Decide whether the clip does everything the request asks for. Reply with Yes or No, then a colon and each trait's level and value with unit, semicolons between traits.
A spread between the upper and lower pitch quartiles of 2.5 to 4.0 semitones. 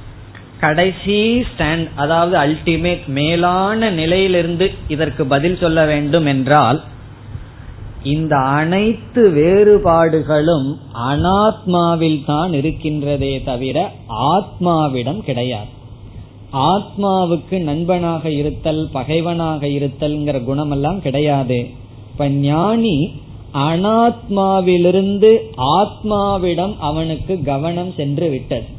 No: average, 4.4 semitones